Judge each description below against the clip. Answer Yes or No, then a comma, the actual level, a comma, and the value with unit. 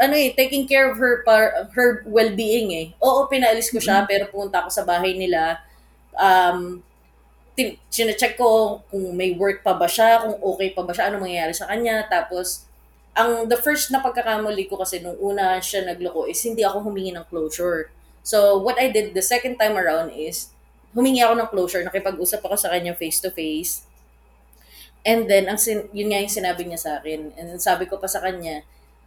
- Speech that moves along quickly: Yes, fast, 190 wpm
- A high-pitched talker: Yes, high, 195 Hz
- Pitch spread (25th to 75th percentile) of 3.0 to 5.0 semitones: Yes, average, 4.6 semitones